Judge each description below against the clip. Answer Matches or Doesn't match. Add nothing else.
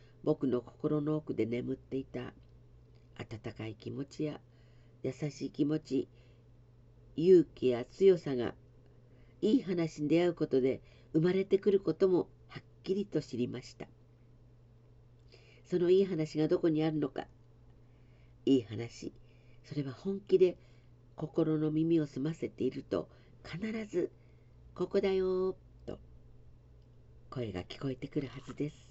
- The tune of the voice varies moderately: Matches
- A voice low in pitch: Matches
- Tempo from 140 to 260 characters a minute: Matches